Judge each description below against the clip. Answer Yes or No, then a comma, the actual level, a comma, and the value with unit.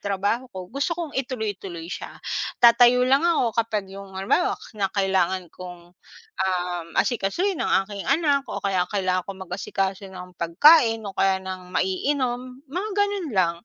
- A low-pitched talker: No, high, 195 Hz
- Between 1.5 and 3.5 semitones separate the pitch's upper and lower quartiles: No, wide, 5.6 semitones